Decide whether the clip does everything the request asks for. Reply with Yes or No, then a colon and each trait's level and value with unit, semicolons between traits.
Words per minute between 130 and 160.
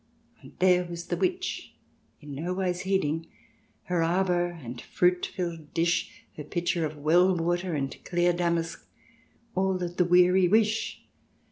Yes: average, 155 wpm